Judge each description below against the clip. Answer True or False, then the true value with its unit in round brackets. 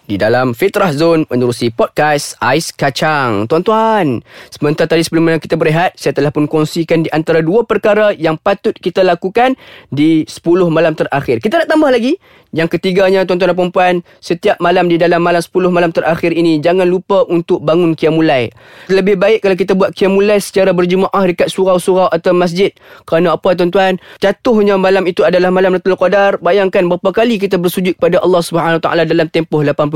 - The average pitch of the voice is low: False (180 Hz)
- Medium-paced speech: False (170 wpm)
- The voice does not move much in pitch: False (3.0 semitones)